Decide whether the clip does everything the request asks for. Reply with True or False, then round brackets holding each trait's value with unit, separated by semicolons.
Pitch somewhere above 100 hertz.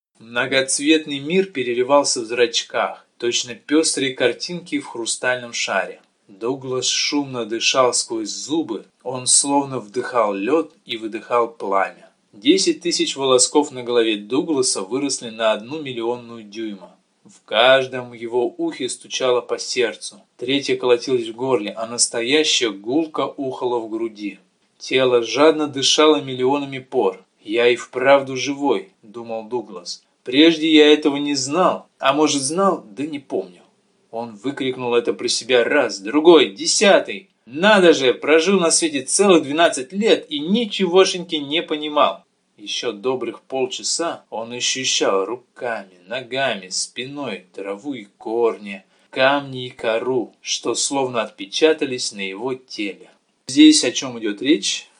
True (140 Hz)